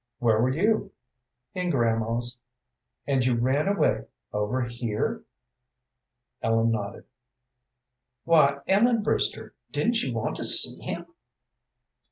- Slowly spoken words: Yes, slow, 110 wpm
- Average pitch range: No, wide, 7.0 semitones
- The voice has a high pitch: No, low, 125 Hz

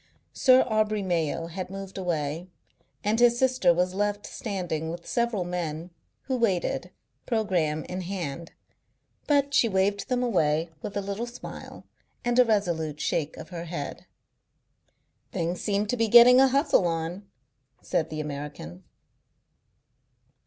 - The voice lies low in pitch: No, high, 190 Hz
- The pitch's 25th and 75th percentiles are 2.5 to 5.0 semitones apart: No, wide, 5.5 semitones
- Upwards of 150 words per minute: No, average, 140 wpm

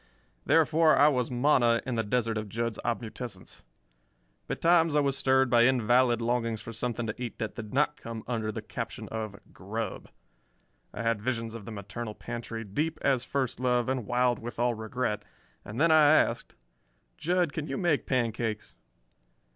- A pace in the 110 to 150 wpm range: No, average, 170 wpm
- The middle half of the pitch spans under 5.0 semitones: Yes, average, 2.8 semitones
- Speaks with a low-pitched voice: Yes, low, 120 Hz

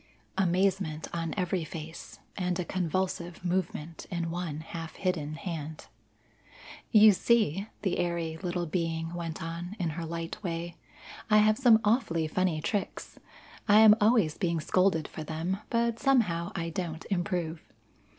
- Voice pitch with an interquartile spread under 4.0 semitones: Yes, average, 2.8 semitones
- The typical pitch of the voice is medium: Yes, medium, 175 Hz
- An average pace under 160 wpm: Yes, average, 140 wpm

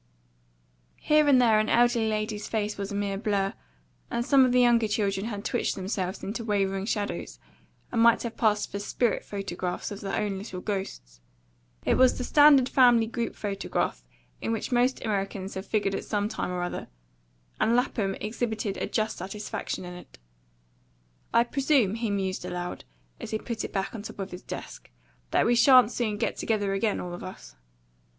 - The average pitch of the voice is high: Yes, high, 210 Hz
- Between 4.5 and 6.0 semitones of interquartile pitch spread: No, average, 3.2 semitones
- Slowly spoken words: No, average, 185 wpm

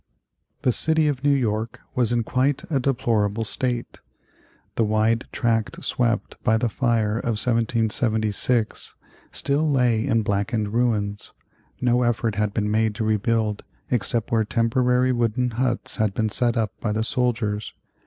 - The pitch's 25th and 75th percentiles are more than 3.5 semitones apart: No, narrow, 2.4 semitones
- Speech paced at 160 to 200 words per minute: No, average, 145 wpm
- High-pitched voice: No, low, 115 Hz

